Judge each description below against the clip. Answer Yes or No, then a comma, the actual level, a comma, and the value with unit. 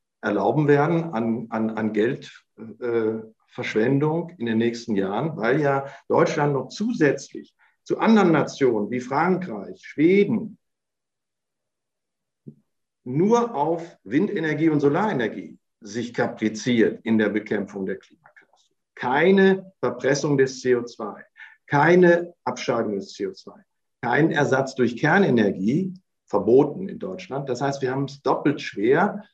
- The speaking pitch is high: No, medium, 140 Hz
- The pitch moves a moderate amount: No, wide, 6.5 semitones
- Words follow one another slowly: Yes, slow, 115 wpm